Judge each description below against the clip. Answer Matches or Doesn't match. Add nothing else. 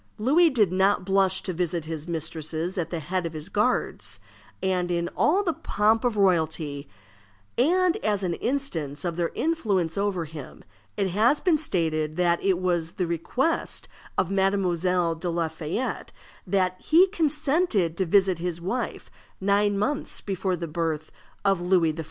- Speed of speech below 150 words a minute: Doesn't match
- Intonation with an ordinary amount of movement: Matches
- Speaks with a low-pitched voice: Doesn't match